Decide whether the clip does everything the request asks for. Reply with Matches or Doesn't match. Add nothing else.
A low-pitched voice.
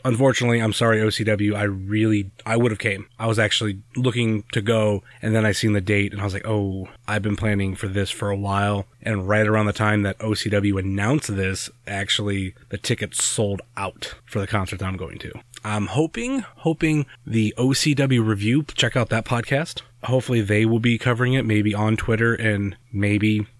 Matches